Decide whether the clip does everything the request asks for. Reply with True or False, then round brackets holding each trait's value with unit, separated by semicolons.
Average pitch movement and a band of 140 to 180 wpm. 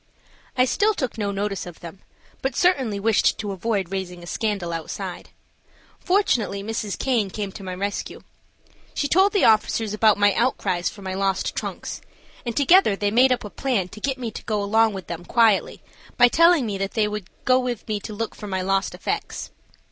False (3.9 semitones; 195 wpm)